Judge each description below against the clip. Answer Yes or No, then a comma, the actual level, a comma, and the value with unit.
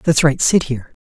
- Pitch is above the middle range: No, medium, 140 Hz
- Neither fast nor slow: No, fast, 230 wpm